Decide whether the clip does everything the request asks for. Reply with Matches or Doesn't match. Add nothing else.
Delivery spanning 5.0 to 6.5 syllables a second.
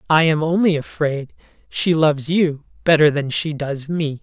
Doesn't match